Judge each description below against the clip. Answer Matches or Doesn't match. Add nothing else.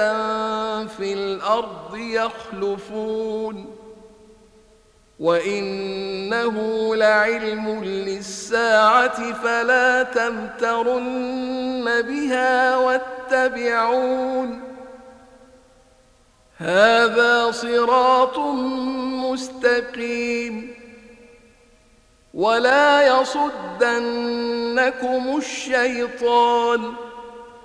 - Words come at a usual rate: Doesn't match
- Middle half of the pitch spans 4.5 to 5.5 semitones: Doesn't match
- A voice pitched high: Matches